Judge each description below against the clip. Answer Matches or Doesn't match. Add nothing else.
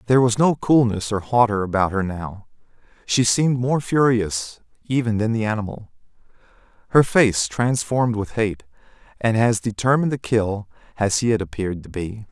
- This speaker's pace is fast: Doesn't match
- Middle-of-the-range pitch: Doesn't match